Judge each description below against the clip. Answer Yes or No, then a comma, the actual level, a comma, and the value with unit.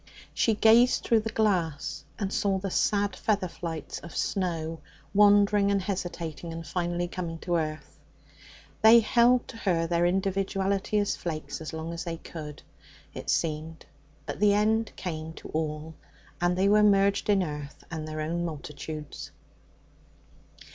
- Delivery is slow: No, average, 150 wpm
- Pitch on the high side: No, medium, 175 Hz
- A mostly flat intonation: No, average, 4.0 semitones